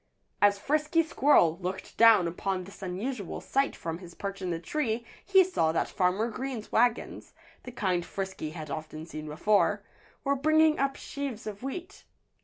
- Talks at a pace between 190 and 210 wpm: No, average, 165 wpm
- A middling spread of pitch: No, wide, 7.3 semitones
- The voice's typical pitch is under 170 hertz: No, high, 205 Hz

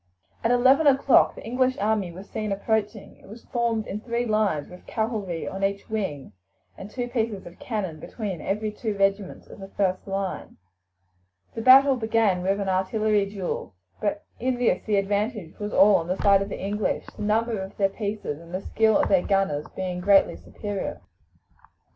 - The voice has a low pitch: No, high, 205 Hz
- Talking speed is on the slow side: No, average, 185 wpm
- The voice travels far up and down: No, narrow, 2.5 semitones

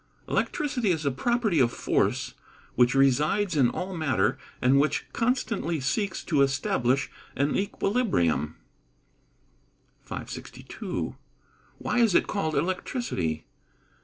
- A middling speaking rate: No, slow, 110 wpm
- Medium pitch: Yes, medium, 155 Hz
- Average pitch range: No, wide, 7.7 semitones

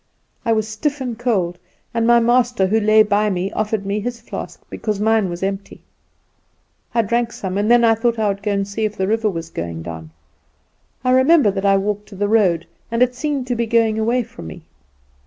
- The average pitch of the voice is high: Yes, high, 215 Hz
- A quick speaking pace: Yes, fast, 215 wpm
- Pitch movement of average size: Yes, average, 3.0 semitones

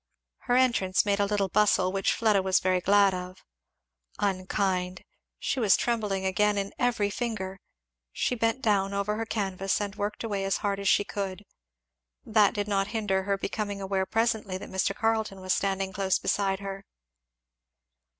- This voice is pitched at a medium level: No, high, 200 Hz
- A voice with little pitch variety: Yes, narrow, 1.7 semitones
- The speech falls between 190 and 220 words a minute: No, average, 165 wpm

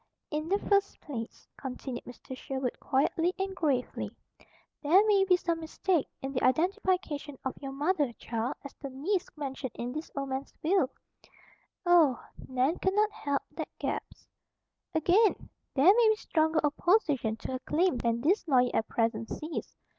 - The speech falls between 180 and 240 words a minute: No, average, 160 wpm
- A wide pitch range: Yes, wide, 5.7 semitones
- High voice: Yes, very high, 295 Hz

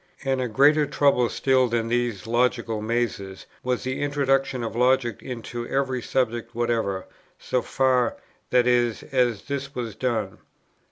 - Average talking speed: Yes, average, 145 wpm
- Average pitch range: No, narrow, 2.2 semitones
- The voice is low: Yes, low, 125 Hz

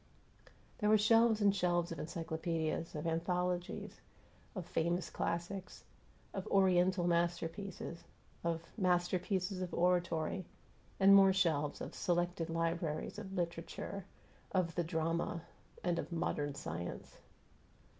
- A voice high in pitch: No, medium, 175 Hz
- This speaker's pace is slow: Yes, slow, 115 wpm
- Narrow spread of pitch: Yes, narrow, 2.0 semitones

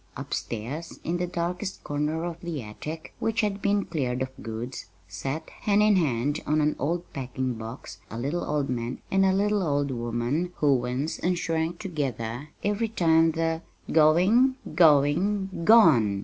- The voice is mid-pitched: Yes, medium, 155 Hz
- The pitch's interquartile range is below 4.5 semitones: No, wide, 5.5 semitones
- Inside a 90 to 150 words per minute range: No, average, 160 wpm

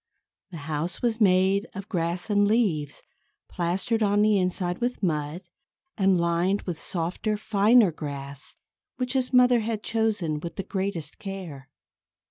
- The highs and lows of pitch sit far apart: No, average, 4.2 semitones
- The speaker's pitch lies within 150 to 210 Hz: Yes, high, 190 Hz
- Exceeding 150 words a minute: No, average, 140 wpm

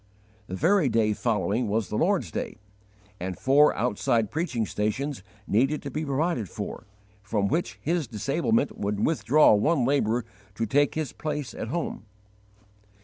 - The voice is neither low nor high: No, low, 125 Hz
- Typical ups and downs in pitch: No, wide, 6.2 semitones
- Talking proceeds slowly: No, average, 145 wpm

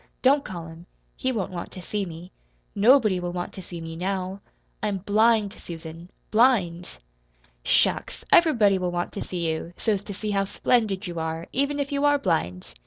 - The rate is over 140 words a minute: Yes, average, 180 wpm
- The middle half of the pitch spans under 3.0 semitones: No, average, 4.2 semitones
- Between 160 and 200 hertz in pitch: Yes, high, 190 Hz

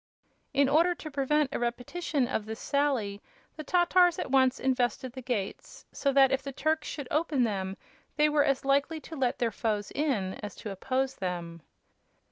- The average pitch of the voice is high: Yes, very high, 270 Hz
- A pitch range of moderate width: Yes, average, 4.6 semitones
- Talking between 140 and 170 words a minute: No, average, 180 wpm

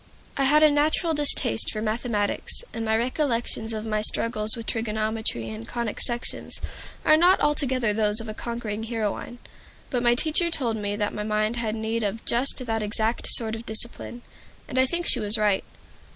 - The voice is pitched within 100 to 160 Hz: No, high, 225 Hz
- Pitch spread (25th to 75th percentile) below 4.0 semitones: Yes, average, 2.7 semitones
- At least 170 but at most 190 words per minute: Yes, average, 180 wpm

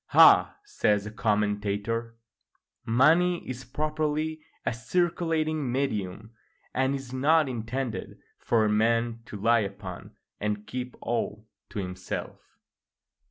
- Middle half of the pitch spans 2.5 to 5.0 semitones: No, wide, 5.4 semitones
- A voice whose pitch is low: Yes, low, 115 Hz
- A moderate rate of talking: No, slow, 115 wpm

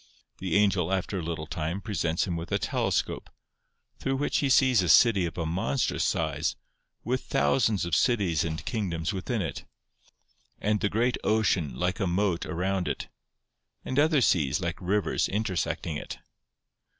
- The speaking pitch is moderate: No, very low, 95 Hz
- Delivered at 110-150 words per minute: No, average, 160 wpm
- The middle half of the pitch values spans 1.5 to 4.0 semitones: No, average, 4.4 semitones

